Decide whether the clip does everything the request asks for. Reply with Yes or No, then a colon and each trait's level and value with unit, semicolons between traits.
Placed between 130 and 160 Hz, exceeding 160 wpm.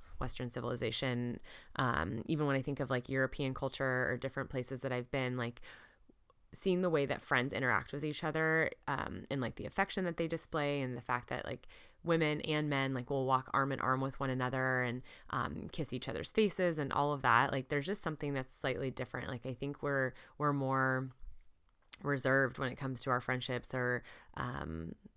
Yes: low, 135 Hz; average, 200 wpm